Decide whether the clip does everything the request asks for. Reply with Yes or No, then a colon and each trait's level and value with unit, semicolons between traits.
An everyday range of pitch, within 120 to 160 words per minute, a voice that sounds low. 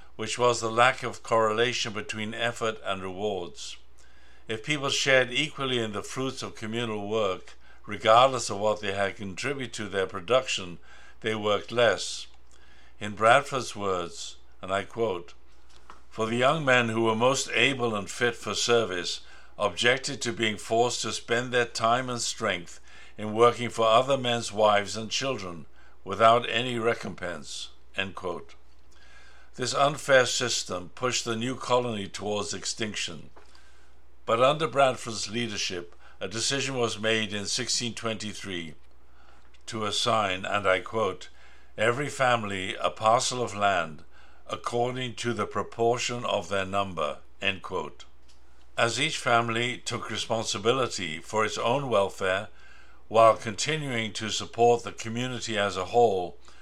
Yes: average, 3.5 semitones; average, 140 wpm; low, 110 Hz